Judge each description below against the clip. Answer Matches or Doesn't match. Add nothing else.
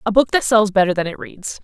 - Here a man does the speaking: Doesn't match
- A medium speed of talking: Doesn't match